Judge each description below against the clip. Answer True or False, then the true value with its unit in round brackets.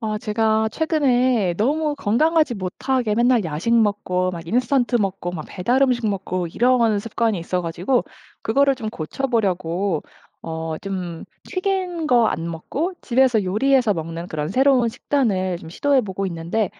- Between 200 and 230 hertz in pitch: True (220 Hz)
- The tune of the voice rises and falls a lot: True (5.9 semitones)